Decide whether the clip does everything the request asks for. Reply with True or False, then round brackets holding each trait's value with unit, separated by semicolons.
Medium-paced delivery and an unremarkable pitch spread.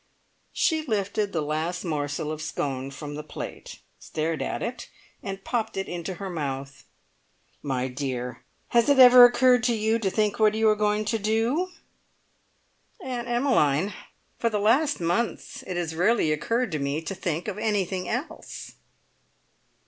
False (155 wpm; 7.0 semitones)